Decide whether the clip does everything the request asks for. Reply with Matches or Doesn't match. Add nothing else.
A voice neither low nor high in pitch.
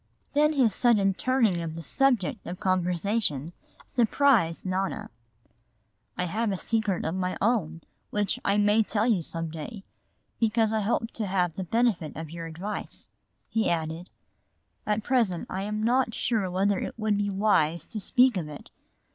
Doesn't match